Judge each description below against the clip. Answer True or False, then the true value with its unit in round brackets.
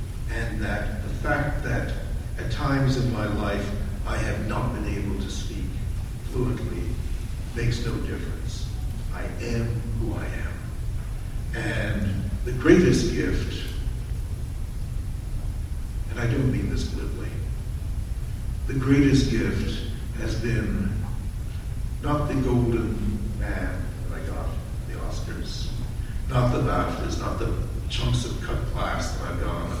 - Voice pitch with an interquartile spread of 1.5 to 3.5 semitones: True (2.7 semitones)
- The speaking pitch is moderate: False (110 Hz)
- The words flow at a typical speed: False (125 wpm)